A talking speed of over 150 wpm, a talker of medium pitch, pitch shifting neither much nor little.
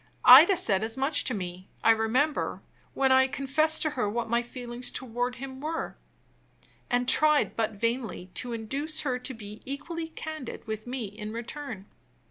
No: average, 165 wpm; very high, 250 Hz; average, 4.3 semitones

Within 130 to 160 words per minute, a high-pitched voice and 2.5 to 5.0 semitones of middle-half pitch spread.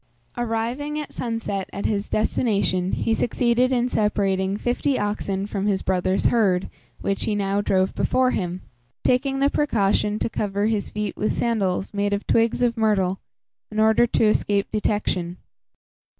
Yes: average, 150 wpm; high, 210 Hz; average, 3.0 semitones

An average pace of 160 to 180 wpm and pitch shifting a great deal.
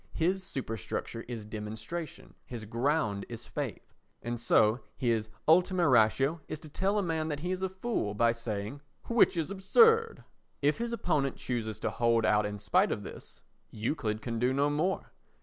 Yes: average, 170 wpm; wide, 7.6 semitones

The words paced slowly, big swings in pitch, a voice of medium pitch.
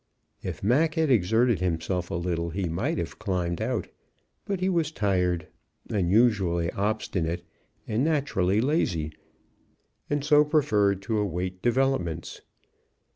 No: slow, 125 wpm; wide, 7.2 semitones; low, 100 Hz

